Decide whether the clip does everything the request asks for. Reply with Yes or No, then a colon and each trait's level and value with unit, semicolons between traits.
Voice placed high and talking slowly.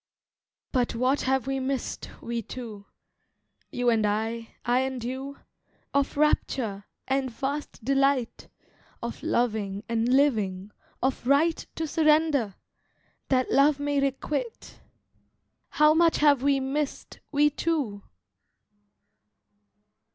Yes: very high, 265 Hz; slow, 105 wpm